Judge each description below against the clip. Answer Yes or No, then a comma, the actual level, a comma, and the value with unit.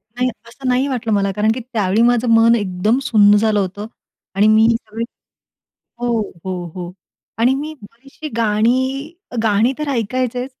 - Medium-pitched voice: No, high, 230 Hz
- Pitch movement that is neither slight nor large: Yes, average, 3.5 semitones